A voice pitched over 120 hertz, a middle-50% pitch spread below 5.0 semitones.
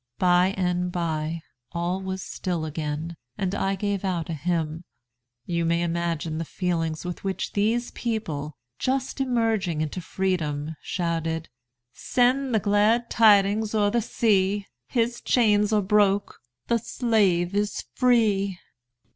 Yes: high, 190 Hz; average, 4.2 semitones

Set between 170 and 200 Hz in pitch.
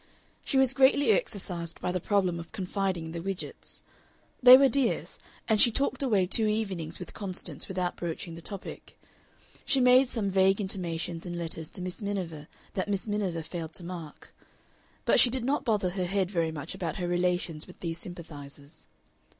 Yes: medium, 185 Hz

